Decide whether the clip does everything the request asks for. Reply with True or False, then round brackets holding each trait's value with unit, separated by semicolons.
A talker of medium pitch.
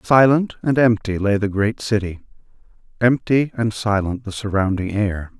False (110 Hz)